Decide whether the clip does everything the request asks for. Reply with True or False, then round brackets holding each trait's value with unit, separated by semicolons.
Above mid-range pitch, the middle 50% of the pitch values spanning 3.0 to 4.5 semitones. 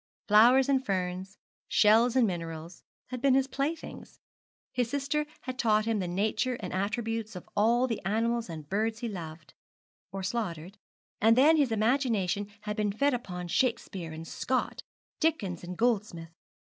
False (215 Hz; 5.0 semitones)